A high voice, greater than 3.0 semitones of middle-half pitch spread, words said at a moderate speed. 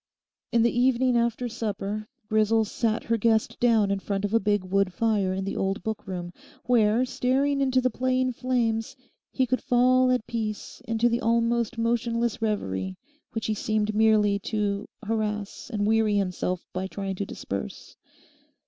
No: high, 220 Hz; average, 2.7 semitones; average, 165 wpm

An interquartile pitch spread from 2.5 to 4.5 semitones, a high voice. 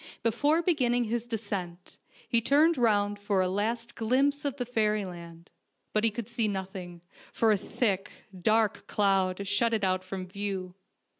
Yes: average, 3.8 semitones; high, 210 Hz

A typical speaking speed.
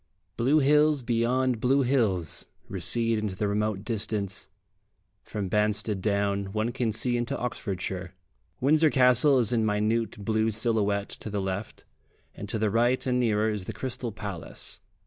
Yes: average, 150 wpm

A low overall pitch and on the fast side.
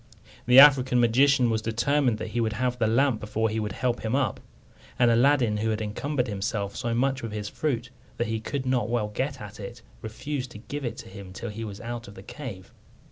Yes: low, 115 Hz; fast, 225 wpm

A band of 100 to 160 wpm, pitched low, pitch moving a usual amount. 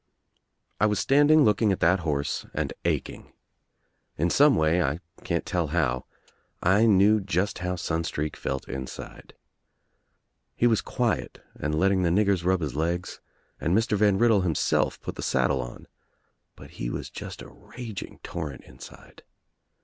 Yes: average, 155 wpm; very low, 90 Hz; average, 4.9 semitones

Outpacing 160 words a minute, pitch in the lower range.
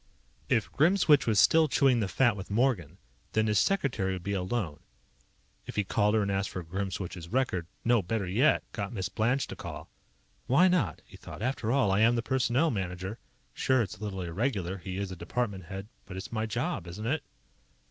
Yes: average, 200 wpm; low, 105 Hz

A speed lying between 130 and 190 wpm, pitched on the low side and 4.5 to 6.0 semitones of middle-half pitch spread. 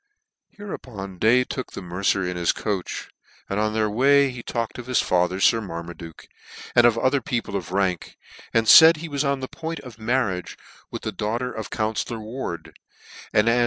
No: average, 200 wpm; low, 110 Hz; average, 4.8 semitones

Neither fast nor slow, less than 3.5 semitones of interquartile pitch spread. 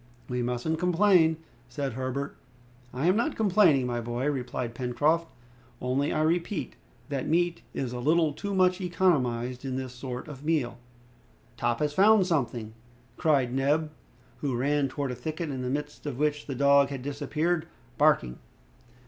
No: average, 155 wpm; average, 4.3 semitones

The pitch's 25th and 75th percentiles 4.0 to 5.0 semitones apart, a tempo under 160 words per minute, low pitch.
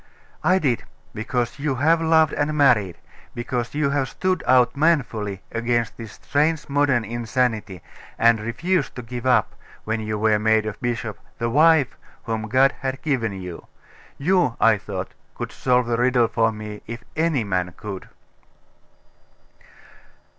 Yes: average, 4.3 semitones; average, 145 wpm; low, 120 Hz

